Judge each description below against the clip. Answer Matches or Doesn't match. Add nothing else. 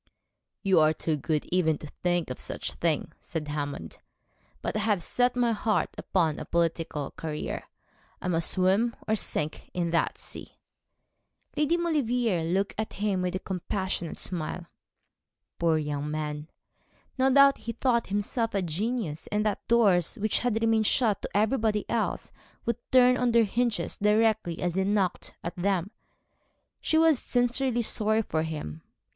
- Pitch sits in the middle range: Doesn't match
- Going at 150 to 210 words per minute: Matches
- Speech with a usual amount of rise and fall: Doesn't match